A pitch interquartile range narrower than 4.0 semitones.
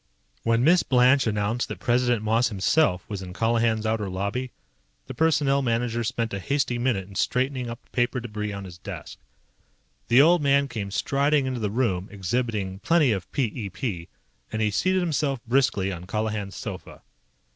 No: average, 4.3 semitones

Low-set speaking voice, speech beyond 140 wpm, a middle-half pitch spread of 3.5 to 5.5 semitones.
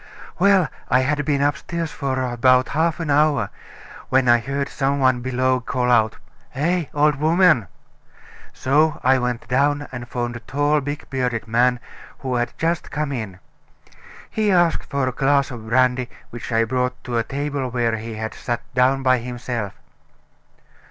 No: low, 130 Hz; average, 160 wpm; average, 3.0 semitones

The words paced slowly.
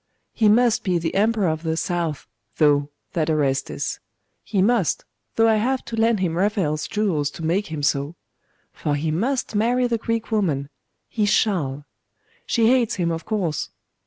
No: average, 165 wpm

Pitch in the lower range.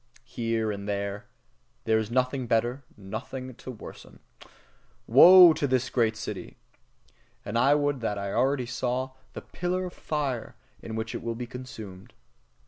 Yes: low, 120 Hz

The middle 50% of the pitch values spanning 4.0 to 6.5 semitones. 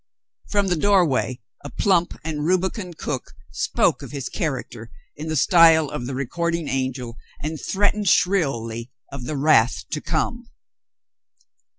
Yes: average, 5.2 semitones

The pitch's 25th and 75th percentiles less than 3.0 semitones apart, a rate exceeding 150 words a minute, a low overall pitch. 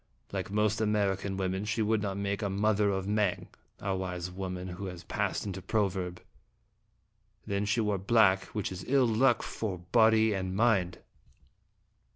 Yes: narrow, 2.4 semitones; average, 170 wpm; low, 100 Hz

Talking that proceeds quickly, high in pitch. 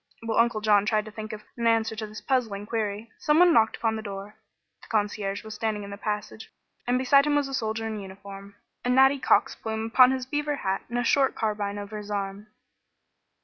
Yes: fast, 215 wpm; high, 220 Hz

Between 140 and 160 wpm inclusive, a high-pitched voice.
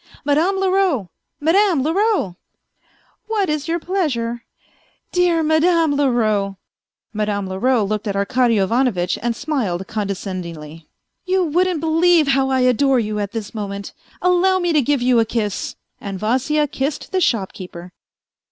Yes: average, 155 wpm; very high, 260 Hz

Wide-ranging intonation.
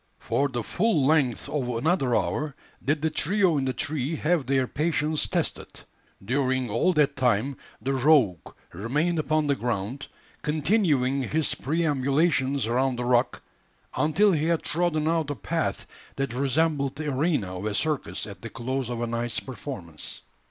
No: average, 4.0 semitones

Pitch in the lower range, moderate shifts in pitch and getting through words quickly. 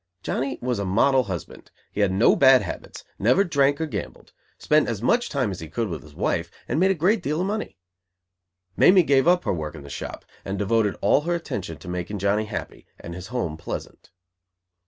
No: low, 115 Hz; wide, 8.2 semitones; fast, 210 wpm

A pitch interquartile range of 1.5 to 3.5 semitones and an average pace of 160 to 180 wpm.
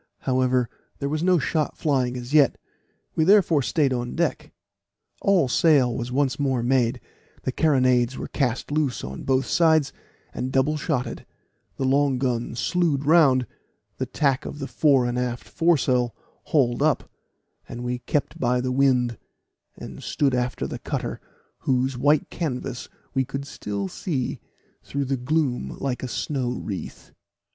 No: average, 3.0 semitones; average, 150 wpm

